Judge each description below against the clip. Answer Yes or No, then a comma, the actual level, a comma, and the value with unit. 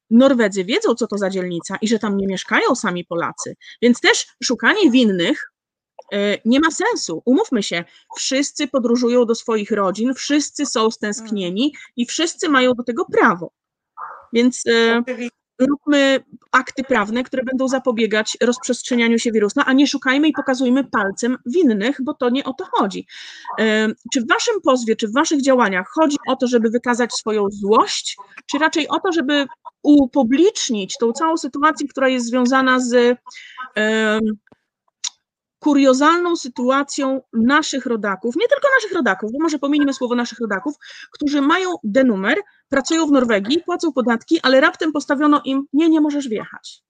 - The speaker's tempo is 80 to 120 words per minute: No, average, 150 wpm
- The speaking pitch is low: No, very high, 260 Hz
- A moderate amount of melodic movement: Yes, average, 4.1 semitones